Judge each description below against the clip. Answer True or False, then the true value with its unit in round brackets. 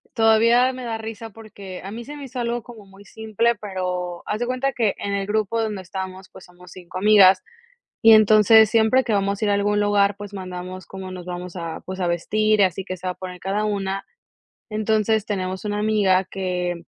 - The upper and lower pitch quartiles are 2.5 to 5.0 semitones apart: True (2.9 semitones)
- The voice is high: True (205 Hz)